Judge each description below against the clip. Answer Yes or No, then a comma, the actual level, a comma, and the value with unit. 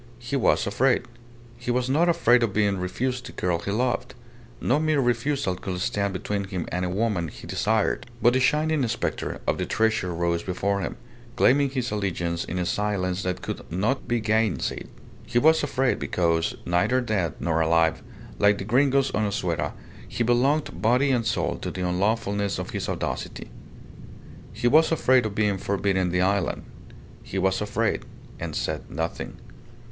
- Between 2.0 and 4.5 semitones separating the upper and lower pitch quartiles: No, average, 5.3 semitones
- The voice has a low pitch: Yes, low, 105 Hz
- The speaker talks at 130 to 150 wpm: No, average, 170 wpm